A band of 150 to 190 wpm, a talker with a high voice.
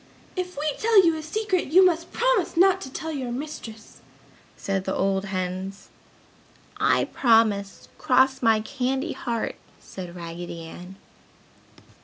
No: slow, 135 wpm; very high, 250 Hz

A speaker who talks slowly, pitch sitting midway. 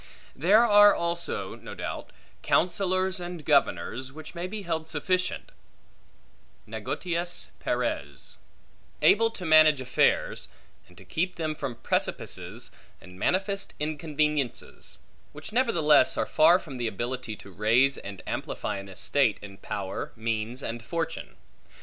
Yes: slow, 125 wpm; medium, 155 Hz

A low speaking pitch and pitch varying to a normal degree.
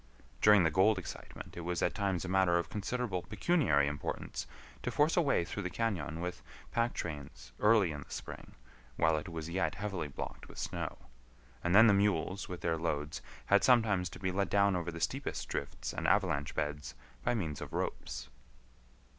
Yes: very low, 90 Hz; average, 4.1 semitones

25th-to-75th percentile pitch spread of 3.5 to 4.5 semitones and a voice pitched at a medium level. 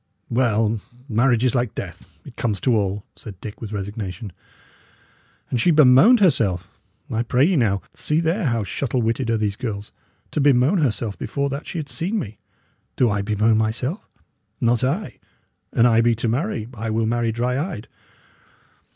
No: average, 4.0 semitones; low, 115 Hz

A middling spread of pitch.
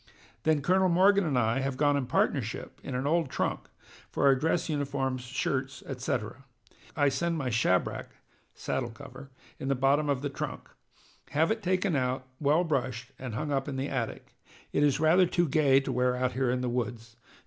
Yes: average, 3.2 semitones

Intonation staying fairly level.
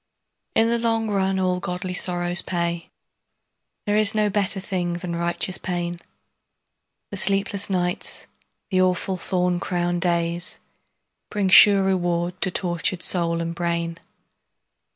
Yes: narrow, 2.0 semitones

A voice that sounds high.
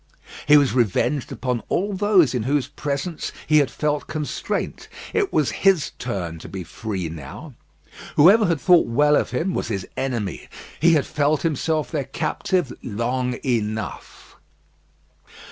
No: medium, 140 Hz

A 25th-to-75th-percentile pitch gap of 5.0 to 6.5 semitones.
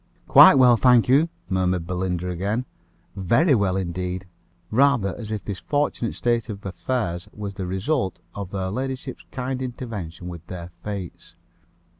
Yes: wide, 5.4 semitones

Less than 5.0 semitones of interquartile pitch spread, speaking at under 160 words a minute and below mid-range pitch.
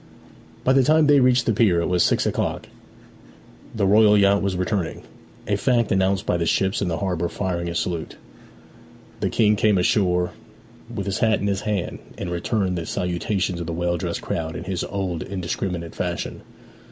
No: average, 3.1 semitones; average, 185 wpm; very low, 95 Hz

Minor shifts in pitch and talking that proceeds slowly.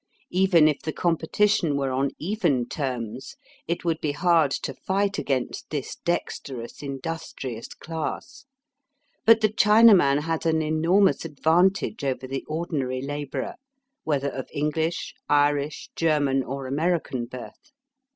No: average, 4.0 semitones; slow, 125 wpm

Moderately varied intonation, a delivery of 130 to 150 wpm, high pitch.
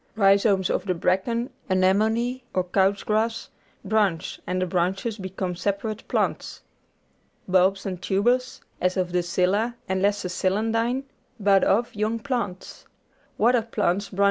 Yes: average, 3.2 semitones; average, 145 wpm; high, 195 Hz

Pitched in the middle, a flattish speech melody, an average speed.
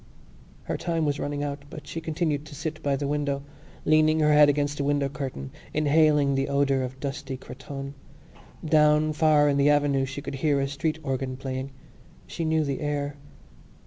Yes: medium, 145 Hz; narrow, 1.7 semitones; average, 180 wpm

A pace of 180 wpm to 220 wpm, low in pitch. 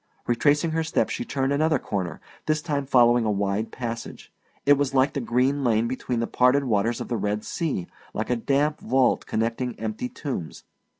Yes: average, 185 wpm; low, 125 Hz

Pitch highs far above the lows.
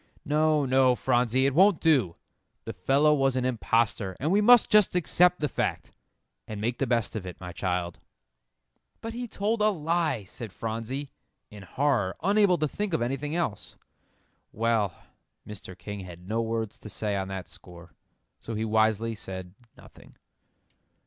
Yes: wide, 6.9 semitones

